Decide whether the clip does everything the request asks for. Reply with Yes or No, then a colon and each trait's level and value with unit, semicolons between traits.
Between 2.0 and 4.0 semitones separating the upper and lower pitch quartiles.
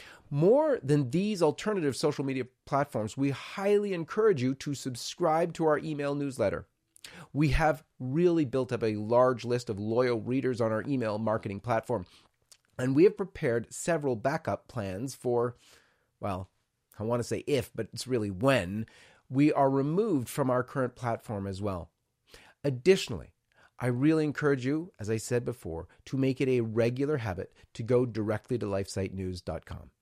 No: average, 4.4 semitones